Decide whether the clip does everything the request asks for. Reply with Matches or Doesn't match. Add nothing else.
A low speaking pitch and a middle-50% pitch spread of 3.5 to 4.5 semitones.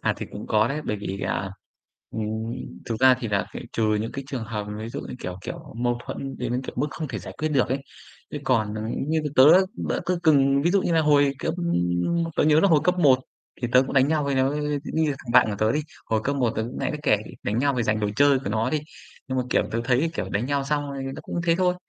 Doesn't match